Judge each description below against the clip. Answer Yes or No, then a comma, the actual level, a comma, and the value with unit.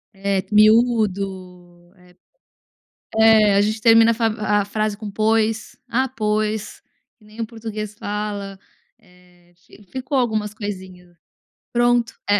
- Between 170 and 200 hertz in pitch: No, high, 210 Hz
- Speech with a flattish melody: Yes, narrow, 2.2 semitones